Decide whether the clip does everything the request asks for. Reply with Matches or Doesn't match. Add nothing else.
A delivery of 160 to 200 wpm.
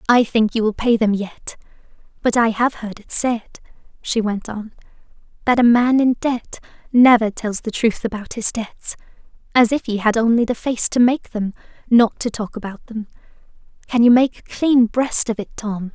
Matches